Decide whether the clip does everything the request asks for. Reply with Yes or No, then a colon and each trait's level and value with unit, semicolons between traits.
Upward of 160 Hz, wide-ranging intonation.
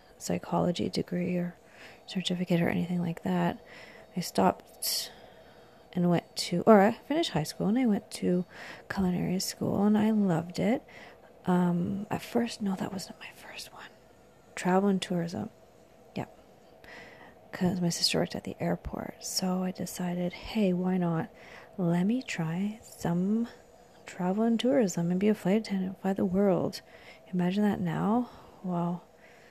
No: medium, 185 Hz; average, 3.2 semitones